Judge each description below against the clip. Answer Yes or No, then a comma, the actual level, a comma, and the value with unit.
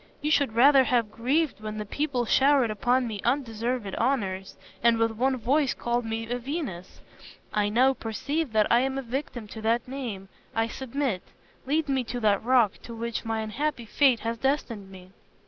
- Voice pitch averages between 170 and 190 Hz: No, high, 235 Hz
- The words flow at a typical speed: Yes, average, 180 wpm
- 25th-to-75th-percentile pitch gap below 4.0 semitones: Yes, average, 3.5 semitones